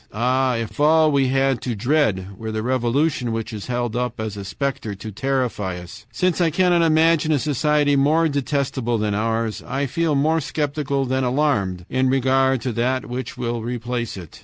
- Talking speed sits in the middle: Yes, average, 185 wpm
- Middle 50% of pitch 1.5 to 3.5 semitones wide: No, average, 4.1 semitones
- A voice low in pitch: Yes, low, 130 Hz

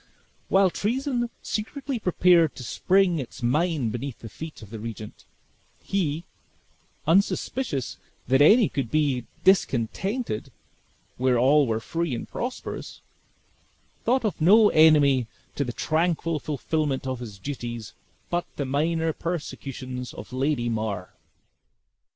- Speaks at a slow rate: Yes, slow, 120 wpm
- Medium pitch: Yes, medium, 150 Hz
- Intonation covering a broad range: Yes, wide, 6.2 semitones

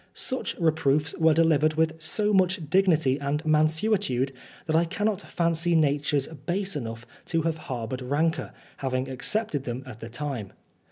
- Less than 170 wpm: Yes, average, 150 wpm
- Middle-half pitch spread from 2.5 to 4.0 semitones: Yes, average, 3.6 semitones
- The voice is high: No, medium, 155 Hz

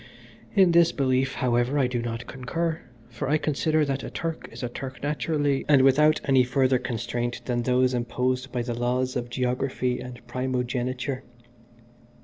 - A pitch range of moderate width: No, narrow, 2.2 semitones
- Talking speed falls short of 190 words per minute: Yes, average, 160 wpm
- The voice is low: Yes, low, 130 Hz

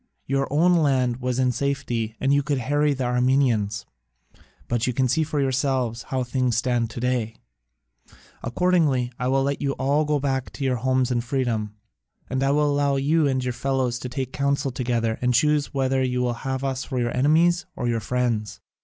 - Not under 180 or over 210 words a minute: Yes, average, 195 wpm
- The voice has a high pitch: No, low, 130 Hz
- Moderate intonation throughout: No, narrow, 2.3 semitones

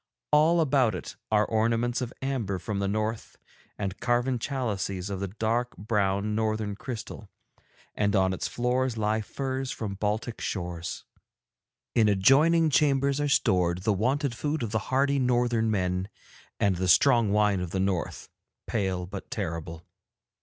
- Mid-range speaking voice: No, low, 110 Hz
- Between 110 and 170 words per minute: Yes, average, 150 wpm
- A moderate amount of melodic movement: Yes, average, 4.4 semitones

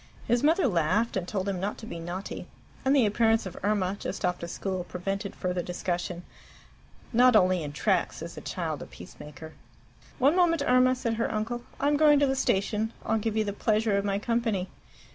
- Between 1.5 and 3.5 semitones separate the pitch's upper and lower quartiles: No, average, 4.6 semitones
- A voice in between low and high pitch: No, high, 210 Hz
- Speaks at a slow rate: No, average, 200 wpm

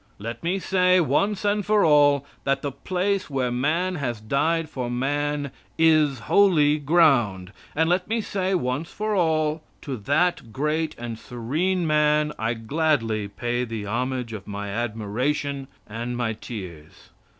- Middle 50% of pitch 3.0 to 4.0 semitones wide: No, wide, 5.5 semitones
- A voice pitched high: No, medium, 145 Hz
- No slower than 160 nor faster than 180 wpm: No, average, 145 wpm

